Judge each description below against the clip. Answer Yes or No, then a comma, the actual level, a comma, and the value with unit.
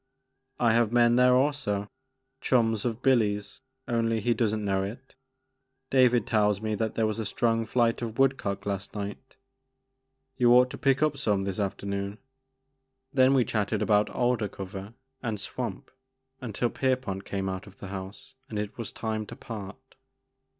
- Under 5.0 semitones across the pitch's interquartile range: Yes, average, 3.5 semitones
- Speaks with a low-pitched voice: Yes, low, 110 Hz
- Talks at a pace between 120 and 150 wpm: No, average, 170 wpm